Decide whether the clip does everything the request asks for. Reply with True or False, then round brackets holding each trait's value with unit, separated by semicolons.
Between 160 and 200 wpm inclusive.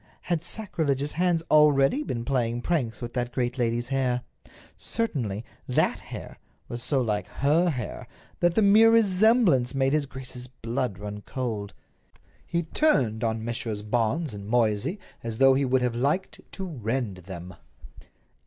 False (150 wpm)